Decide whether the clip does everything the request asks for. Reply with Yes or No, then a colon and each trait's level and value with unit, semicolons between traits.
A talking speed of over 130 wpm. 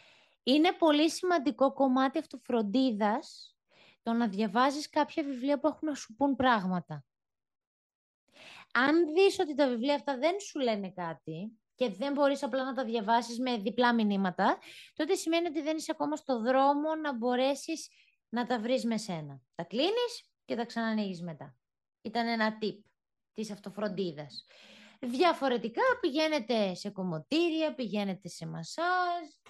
Yes: average, 140 wpm